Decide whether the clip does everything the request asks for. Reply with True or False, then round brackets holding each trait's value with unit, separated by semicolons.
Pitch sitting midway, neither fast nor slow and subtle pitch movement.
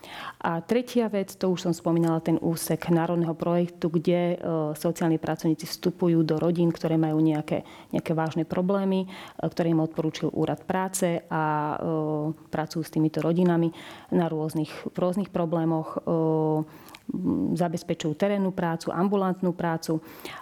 True (165 Hz; 130 wpm; 1.7 semitones)